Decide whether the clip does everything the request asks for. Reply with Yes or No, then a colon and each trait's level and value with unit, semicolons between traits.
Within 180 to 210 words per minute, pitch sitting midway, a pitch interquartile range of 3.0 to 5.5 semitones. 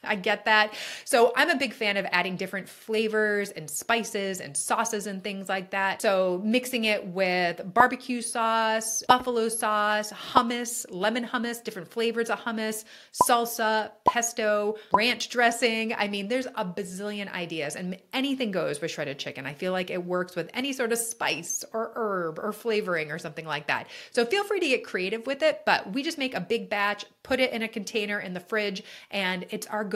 No: average, 190 wpm; high, 215 Hz; average, 3.5 semitones